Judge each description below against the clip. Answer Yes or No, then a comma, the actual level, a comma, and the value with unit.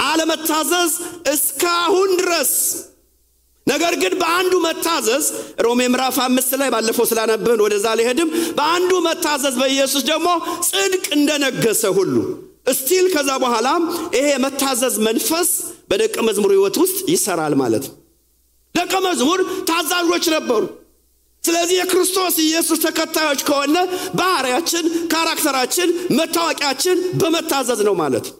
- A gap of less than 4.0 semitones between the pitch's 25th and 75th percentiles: No, average, 4.3 semitones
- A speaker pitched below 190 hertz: No, very high, 335 Hz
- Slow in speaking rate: Yes, slow, 105 wpm